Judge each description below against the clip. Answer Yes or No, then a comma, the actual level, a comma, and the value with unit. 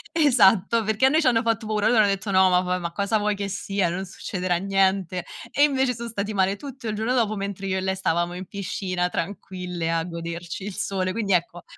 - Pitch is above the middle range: Yes, high, 195 Hz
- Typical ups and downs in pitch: Yes, average, 3.1 semitones